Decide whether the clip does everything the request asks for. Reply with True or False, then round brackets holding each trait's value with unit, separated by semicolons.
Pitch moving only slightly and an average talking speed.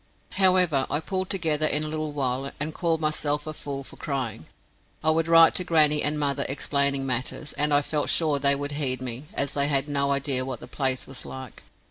False (2.1 semitones; 210 wpm)